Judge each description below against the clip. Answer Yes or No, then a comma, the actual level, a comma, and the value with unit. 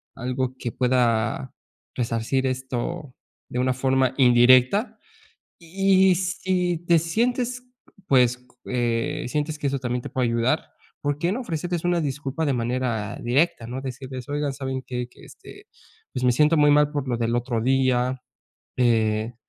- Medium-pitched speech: No, low, 130 Hz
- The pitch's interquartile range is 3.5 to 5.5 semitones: Yes, average, 3.8 semitones